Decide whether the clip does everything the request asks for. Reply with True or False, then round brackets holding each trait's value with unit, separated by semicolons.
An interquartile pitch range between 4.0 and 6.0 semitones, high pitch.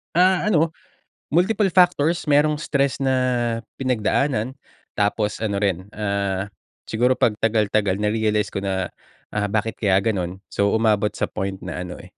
False (5.1 semitones; 110 Hz)